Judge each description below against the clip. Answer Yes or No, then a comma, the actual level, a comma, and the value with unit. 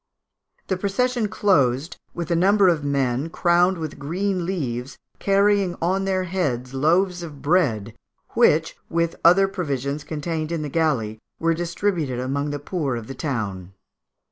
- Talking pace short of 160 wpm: Yes, average, 145 wpm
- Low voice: No, medium, 165 Hz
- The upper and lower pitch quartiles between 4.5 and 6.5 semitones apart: Yes, average, 5.1 semitones